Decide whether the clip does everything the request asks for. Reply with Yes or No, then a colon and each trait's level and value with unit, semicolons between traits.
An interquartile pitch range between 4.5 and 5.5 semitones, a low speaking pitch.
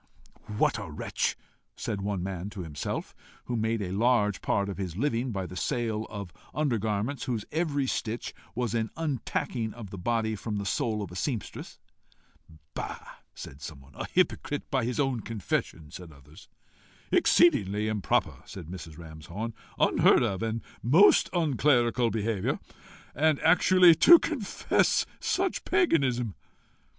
Yes: average, 5.2 semitones; low, 110 Hz